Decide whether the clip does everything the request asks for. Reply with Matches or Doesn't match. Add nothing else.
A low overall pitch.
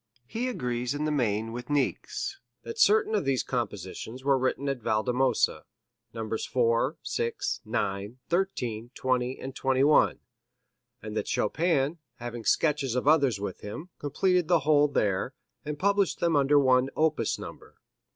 Matches